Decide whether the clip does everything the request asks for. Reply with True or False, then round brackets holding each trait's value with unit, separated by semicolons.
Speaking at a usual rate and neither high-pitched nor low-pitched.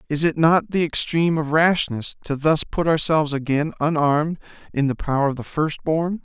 True (190 wpm; 155 Hz)